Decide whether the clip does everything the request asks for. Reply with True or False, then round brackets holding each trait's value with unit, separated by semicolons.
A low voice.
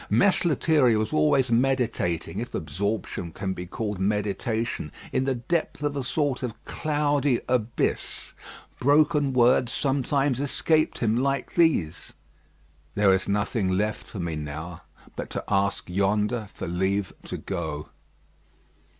True (115 Hz)